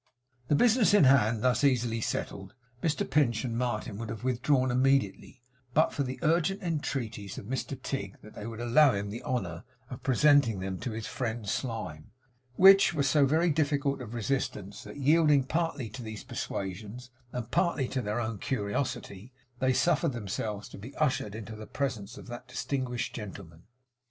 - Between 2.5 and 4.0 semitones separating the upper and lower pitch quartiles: No, average, 4.7 semitones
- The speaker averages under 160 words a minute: No, average, 170 wpm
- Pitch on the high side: No, low, 125 Hz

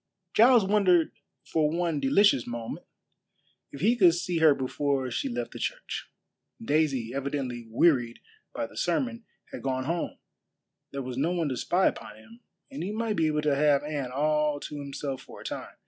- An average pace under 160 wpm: No, average, 180 wpm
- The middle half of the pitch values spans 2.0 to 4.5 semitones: No, average, 4.9 semitones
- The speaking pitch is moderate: Yes, medium, 150 Hz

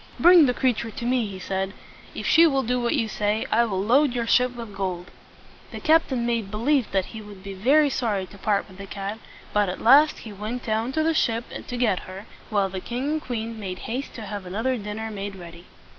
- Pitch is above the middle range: Yes, high, 220 Hz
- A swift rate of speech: Yes, fast, 230 wpm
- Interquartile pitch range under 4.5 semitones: Yes, average, 4.0 semitones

